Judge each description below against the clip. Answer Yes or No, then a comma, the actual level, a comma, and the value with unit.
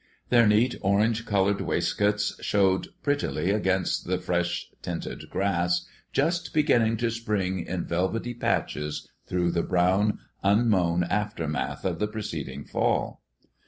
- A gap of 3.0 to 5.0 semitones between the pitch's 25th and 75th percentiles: Yes, average, 3.6 semitones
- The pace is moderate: No, slow, 125 wpm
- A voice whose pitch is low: Yes, very low, 95 Hz